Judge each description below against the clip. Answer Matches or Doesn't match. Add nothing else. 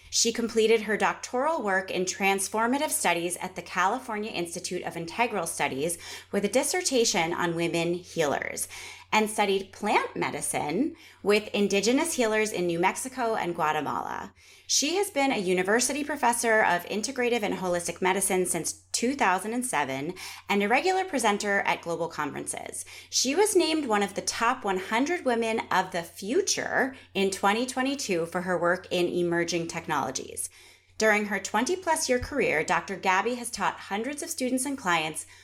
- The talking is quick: Doesn't match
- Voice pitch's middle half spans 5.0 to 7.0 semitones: Matches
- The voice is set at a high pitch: Matches